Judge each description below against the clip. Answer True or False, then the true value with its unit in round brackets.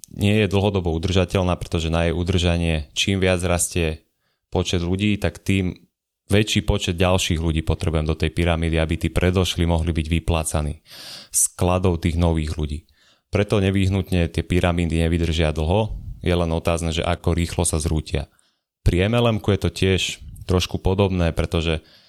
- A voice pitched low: True (85 Hz)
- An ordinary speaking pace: True (150 wpm)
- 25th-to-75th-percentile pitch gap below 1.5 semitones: False (2.5 semitones)